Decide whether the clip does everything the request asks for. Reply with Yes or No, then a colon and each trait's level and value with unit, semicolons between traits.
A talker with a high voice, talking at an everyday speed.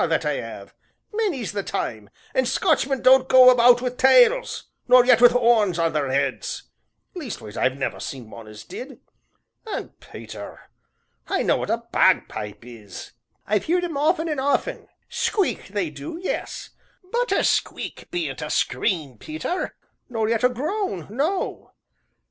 Yes: high, 245 Hz; average, 155 wpm